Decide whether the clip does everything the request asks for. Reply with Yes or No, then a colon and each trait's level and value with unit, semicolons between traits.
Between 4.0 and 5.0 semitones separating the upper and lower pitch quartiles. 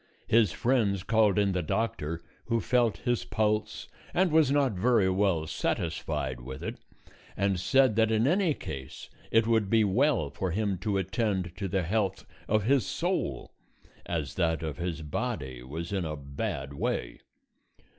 No: wide, 5.5 semitones